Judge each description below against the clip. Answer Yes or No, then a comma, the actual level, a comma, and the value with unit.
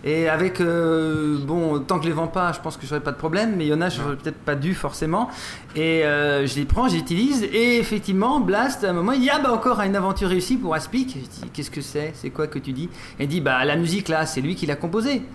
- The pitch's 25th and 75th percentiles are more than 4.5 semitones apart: Yes, average, 4.9 semitones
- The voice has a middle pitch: Yes, medium, 165 Hz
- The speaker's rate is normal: No, fast, 280 wpm